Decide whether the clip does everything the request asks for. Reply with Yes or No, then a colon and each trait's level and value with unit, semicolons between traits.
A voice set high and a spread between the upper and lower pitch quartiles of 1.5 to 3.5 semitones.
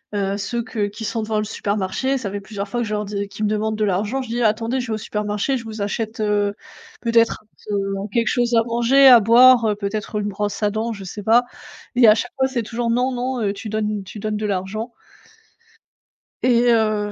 Yes: high, 215 Hz; narrow, 2.4 semitones